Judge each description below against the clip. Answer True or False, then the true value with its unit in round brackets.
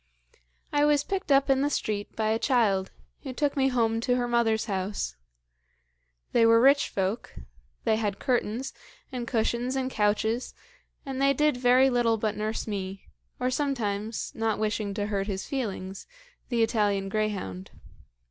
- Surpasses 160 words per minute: False (155 wpm)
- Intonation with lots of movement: False (3.8 semitones)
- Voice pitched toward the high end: True (225 Hz)